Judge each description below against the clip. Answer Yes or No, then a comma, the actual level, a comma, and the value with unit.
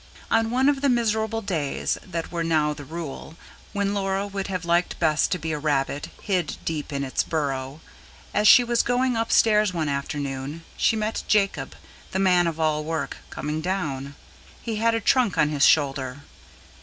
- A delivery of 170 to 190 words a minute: Yes, average, 180 wpm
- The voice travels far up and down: Yes, wide, 6.1 semitones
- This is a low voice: No, medium, 170 Hz